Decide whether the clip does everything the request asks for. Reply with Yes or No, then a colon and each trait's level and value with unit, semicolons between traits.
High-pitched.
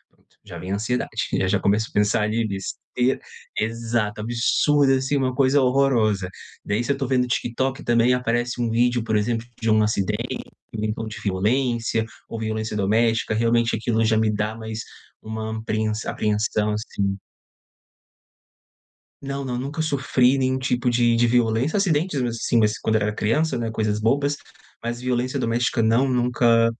No: low, 115 Hz